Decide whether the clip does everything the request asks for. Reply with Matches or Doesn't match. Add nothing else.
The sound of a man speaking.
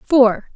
Doesn't match